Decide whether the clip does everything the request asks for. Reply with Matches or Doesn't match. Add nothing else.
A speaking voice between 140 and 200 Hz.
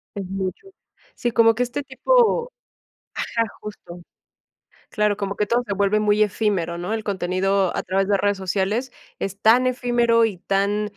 Doesn't match